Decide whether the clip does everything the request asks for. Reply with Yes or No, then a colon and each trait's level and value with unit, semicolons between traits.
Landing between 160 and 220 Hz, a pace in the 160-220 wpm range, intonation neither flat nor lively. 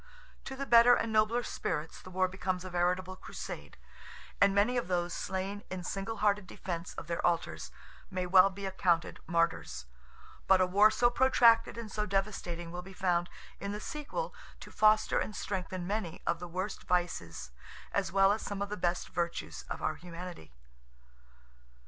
Yes: medium, 185 Hz; average, 170 wpm; average, 3.1 semitones